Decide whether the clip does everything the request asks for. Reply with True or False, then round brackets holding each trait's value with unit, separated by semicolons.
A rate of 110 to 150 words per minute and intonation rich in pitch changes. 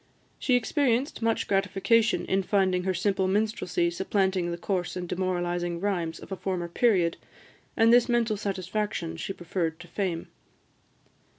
False (140 wpm; 3.2 semitones)